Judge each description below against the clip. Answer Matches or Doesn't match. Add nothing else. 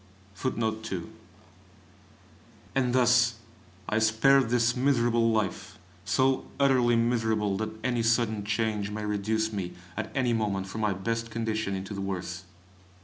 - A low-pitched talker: Matches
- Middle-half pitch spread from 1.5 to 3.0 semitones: Matches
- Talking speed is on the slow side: Matches